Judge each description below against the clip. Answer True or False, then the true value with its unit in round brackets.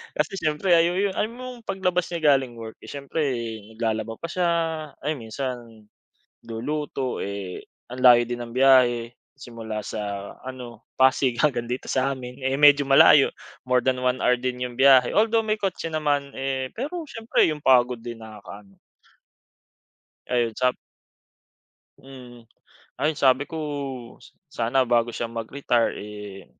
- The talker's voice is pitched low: True (130 Hz)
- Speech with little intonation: False (3.6 semitones)